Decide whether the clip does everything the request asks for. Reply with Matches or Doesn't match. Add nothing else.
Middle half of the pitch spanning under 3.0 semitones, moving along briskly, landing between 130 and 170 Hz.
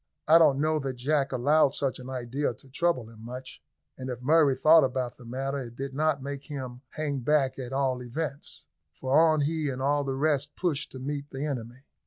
Matches